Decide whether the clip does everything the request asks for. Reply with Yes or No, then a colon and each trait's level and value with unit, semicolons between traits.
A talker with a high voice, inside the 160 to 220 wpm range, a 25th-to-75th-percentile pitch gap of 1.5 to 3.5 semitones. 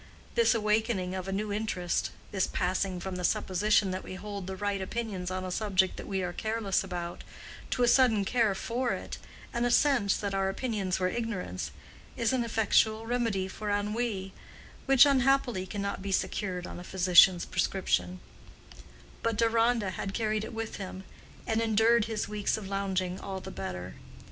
Yes: high, 200 Hz; average, 165 wpm; average, 3.2 semitones